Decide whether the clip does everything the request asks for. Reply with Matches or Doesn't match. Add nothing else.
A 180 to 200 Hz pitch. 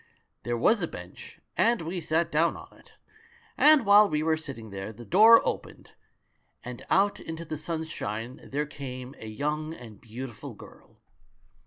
Doesn't match